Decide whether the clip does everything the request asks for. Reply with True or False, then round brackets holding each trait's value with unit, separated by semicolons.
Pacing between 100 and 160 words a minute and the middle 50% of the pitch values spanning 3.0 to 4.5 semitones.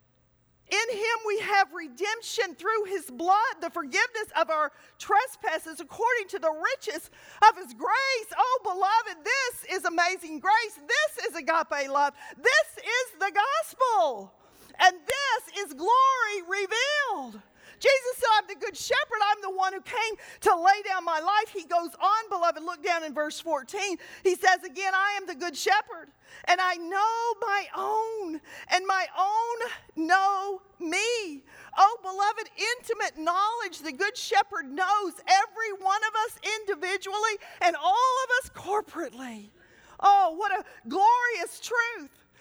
True (150 wpm; 3.9 semitones)